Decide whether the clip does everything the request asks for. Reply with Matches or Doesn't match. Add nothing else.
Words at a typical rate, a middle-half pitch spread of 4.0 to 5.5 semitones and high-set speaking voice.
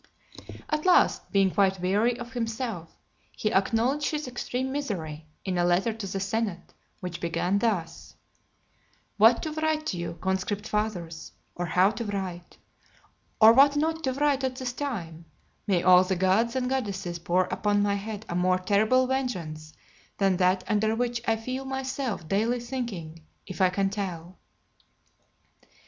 Matches